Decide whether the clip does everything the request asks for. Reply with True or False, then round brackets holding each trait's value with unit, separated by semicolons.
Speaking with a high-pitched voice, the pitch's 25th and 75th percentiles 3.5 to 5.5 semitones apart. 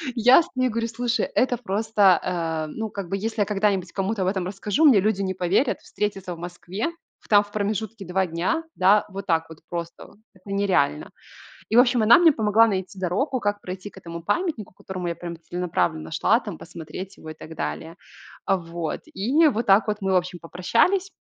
True (195 Hz; 3.8 semitones)